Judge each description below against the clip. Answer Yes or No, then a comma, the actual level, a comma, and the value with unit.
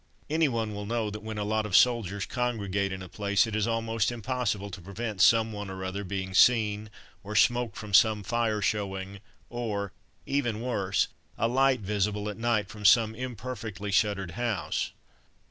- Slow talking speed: No, average, 165 wpm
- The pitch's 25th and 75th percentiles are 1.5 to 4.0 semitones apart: Yes, narrow, 2.6 semitones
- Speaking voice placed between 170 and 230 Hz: No, low, 105 Hz